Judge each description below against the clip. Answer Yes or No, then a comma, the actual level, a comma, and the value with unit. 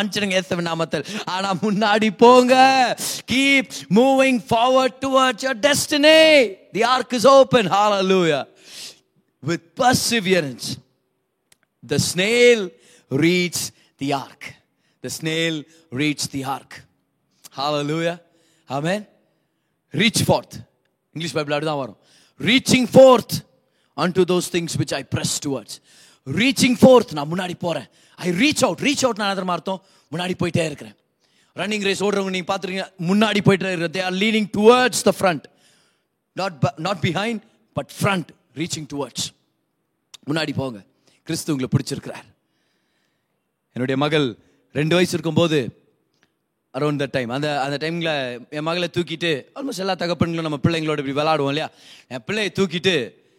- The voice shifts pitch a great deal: Yes, wide, 6.0 semitones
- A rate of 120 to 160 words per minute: No, average, 100 wpm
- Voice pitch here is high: No, medium, 175 Hz